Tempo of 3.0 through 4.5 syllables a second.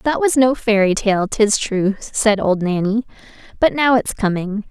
Yes: 4.2 syllables/s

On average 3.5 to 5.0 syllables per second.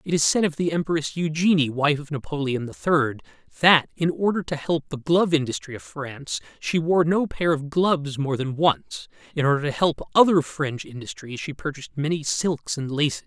No: 5.2 syllables/s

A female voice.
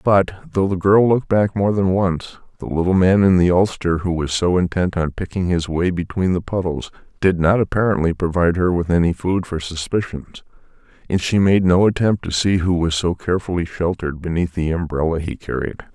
No: male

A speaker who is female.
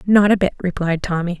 Yes: female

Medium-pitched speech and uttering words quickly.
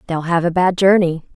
Yes: medium, 175 Hz; fast, 220 wpm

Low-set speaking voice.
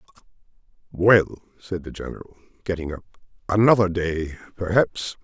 Yes: very low, 95 Hz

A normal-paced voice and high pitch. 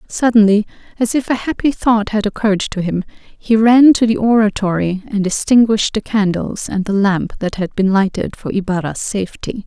Yes: average, 180 wpm; high, 210 Hz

